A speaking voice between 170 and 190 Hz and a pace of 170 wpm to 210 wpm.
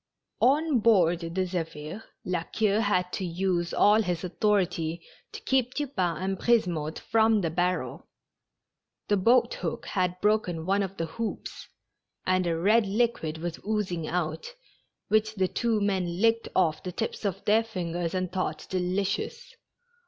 No: medium, 185 Hz; average, 150 wpm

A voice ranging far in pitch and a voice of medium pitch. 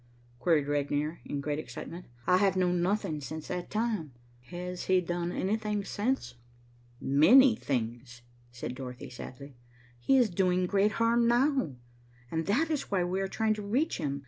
Yes: wide, 6.5 semitones; medium, 180 Hz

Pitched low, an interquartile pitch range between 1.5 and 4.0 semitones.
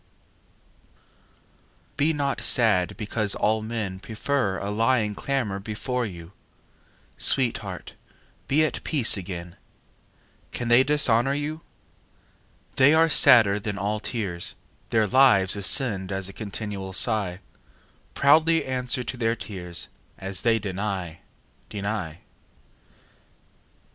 No: low, 110 Hz; average, 4.8 semitones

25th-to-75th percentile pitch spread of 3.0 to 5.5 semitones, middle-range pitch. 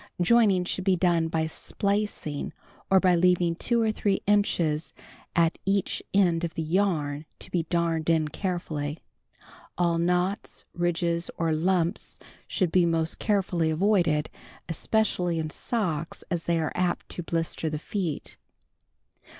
No: narrow, 2.6 semitones; medium, 170 Hz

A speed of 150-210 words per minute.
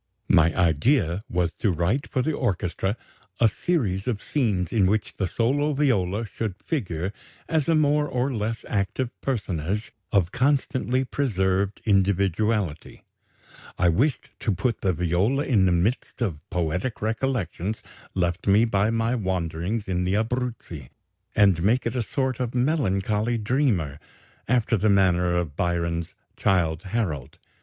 No: average, 140 wpm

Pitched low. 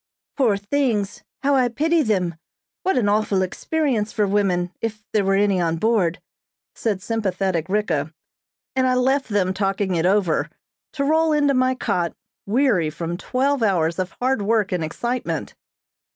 No: high, 205 Hz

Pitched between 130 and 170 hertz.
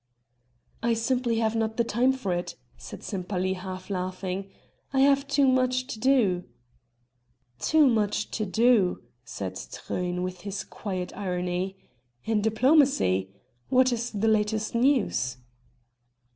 No: high, 215 Hz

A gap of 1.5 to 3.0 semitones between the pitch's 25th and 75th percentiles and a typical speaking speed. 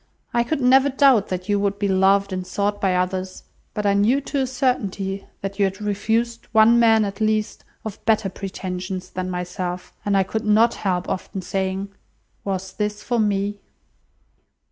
Yes: narrow, 2.6 semitones; average, 175 wpm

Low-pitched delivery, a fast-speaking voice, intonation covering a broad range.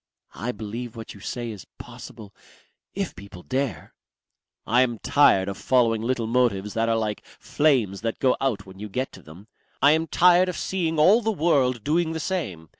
No: low, 120 Hz; average, 190 wpm; wide, 6.1 semitones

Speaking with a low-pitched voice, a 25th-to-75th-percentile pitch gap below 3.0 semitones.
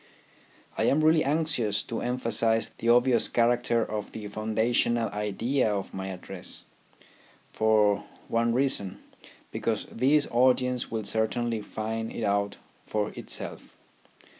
Yes: low, 115 Hz; narrow, 2.5 semitones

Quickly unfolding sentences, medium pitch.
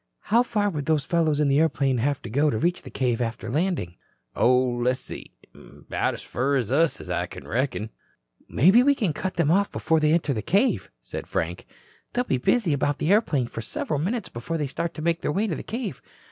Yes: fast, 215 wpm; medium, 150 Hz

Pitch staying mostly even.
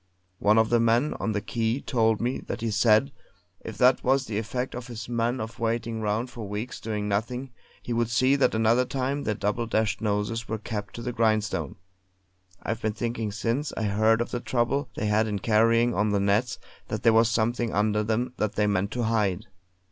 Yes: narrow, 2.0 semitones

